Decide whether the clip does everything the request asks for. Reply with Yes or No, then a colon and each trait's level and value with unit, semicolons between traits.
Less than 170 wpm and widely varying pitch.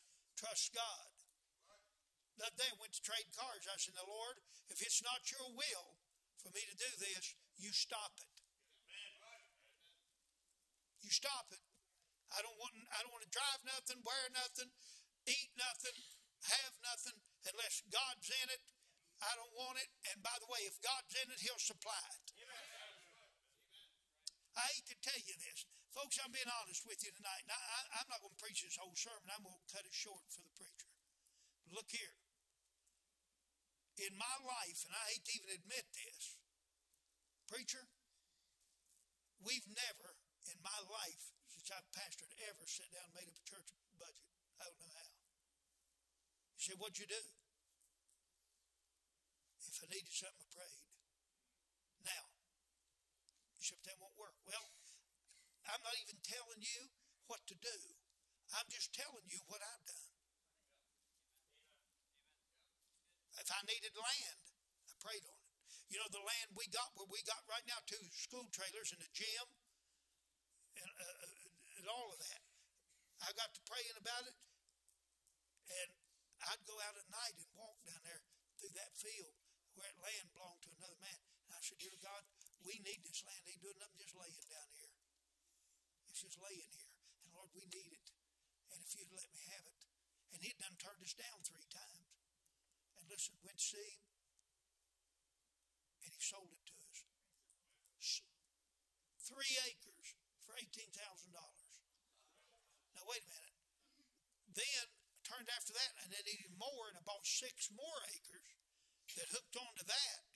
Yes: average, 160 wpm; wide, 6.1 semitones